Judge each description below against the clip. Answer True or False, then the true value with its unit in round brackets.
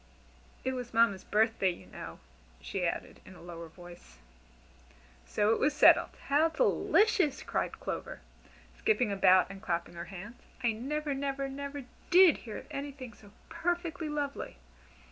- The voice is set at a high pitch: True (250 Hz)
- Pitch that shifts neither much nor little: False (7.0 semitones)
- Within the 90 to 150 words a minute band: True (145 wpm)